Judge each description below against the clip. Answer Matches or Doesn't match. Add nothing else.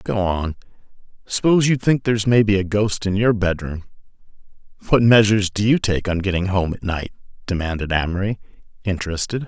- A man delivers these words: Matches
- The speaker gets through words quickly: Doesn't match